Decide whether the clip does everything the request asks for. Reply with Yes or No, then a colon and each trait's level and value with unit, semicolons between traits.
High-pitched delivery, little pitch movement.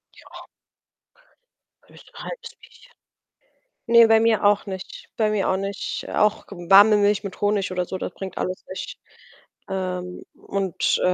Yes: high, 200 Hz; narrow, 2.1 semitones